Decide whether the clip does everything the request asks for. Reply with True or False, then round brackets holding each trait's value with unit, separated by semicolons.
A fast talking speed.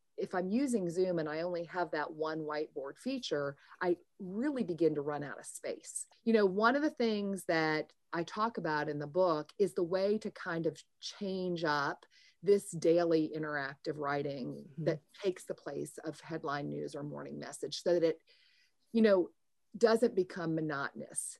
False (175 wpm)